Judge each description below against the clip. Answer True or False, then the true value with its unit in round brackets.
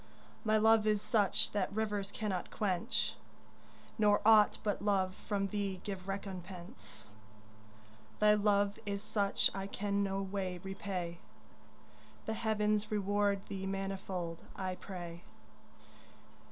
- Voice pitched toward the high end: True (200 Hz)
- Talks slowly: True (115 wpm)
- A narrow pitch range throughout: True (1.7 semitones)